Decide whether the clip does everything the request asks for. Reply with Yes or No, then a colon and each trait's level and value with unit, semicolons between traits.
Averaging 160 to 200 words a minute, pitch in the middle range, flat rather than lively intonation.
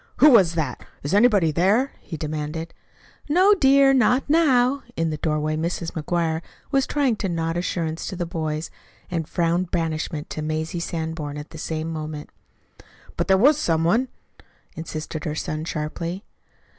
No: average, 165 wpm; medium, 165 Hz; average, 4.9 semitones